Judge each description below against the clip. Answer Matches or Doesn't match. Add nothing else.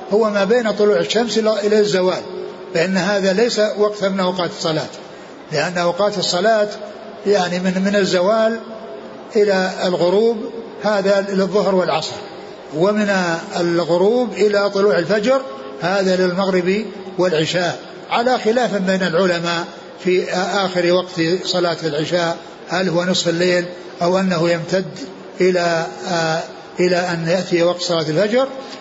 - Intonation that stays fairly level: Doesn't match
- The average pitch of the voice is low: Doesn't match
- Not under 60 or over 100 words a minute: Doesn't match